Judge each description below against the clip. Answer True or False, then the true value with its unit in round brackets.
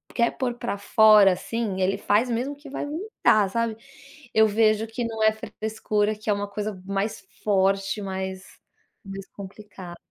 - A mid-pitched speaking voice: False (215 Hz)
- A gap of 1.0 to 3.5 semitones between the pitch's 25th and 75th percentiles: True (2.4 semitones)